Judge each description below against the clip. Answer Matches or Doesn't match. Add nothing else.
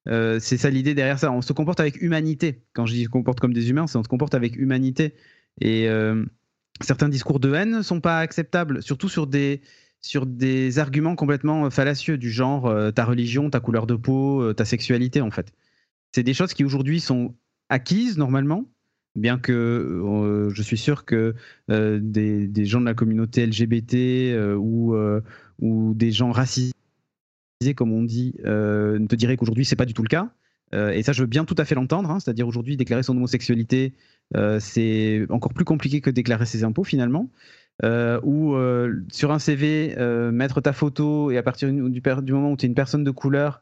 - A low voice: Matches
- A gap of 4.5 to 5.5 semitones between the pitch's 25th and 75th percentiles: Doesn't match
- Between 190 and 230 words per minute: Matches